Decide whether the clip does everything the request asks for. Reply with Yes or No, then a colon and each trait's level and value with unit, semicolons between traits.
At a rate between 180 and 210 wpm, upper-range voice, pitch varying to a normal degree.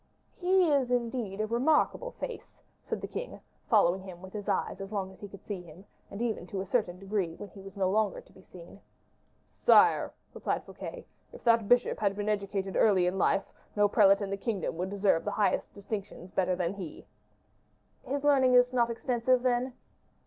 Yes: average, 195 wpm; high, 205 Hz; average, 4.0 semitones